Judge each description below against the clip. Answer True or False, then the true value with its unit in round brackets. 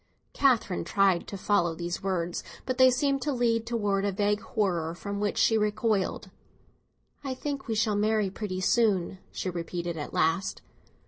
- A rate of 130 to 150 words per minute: False (165 wpm)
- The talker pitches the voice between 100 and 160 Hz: False (205 Hz)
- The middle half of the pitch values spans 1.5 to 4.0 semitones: True (3.7 semitones)